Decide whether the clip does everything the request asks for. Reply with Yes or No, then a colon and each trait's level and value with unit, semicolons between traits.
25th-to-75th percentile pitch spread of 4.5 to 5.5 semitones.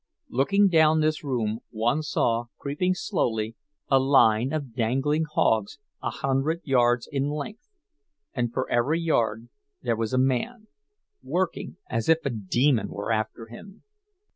Yes: average, 5.1 semitones